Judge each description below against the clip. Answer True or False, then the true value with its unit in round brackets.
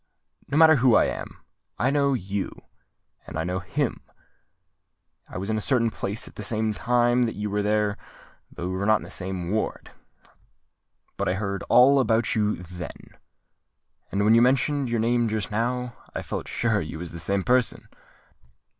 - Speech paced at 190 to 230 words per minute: False (180 wpm)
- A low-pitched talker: True (110 Hz)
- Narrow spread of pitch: False (3.8 semitones)